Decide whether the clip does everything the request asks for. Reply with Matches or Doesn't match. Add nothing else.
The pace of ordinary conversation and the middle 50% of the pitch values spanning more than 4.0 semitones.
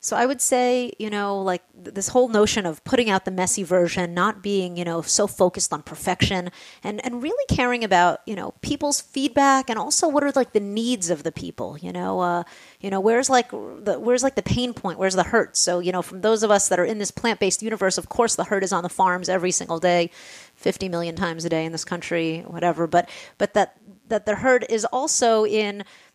Doesn't match